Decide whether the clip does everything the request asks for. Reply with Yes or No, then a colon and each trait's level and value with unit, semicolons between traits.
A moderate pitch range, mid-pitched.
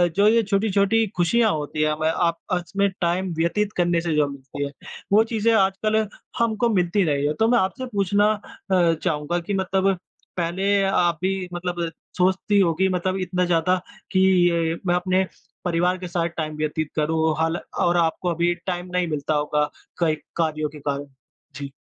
Yes: average, 3.2 semitones; medium, 175 Hz